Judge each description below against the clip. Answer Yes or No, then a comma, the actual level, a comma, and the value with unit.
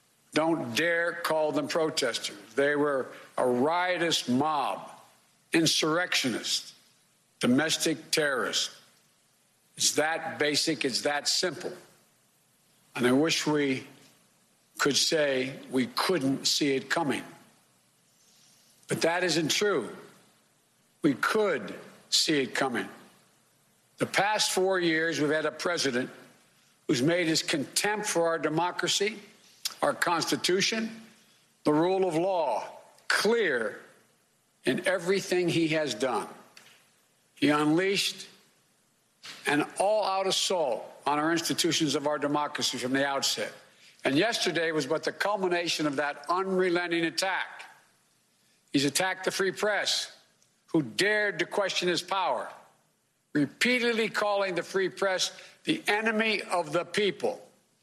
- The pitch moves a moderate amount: Yes, average, 4.2 semitones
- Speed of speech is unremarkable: No, slow, 115 wpm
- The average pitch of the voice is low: No, medium, 170 Hz